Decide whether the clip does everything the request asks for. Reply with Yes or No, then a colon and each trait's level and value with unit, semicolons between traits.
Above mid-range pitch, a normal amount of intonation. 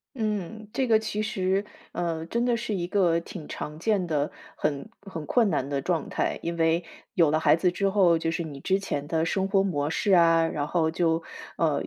No: medium, 170 Hz; average, 3.6 semitones